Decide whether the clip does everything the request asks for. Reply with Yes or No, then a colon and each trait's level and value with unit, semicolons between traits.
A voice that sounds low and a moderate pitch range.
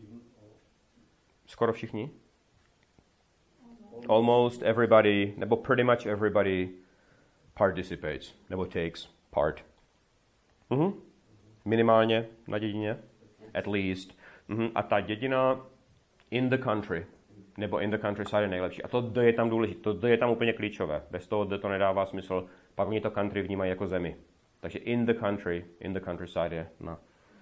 Yes: low, 105 Hz; average, 3.2 semitones